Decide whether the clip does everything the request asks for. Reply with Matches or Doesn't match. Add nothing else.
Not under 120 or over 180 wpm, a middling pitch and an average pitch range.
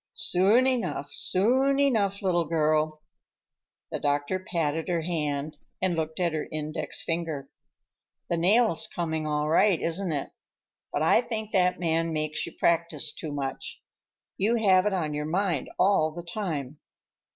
Matches